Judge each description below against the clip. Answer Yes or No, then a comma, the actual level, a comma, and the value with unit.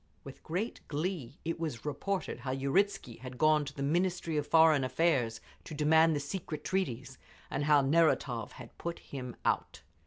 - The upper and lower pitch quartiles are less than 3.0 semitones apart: No, average, 3.8 semitones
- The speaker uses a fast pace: No, average, 165 wpm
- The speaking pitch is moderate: Yes, medium, 150 Hz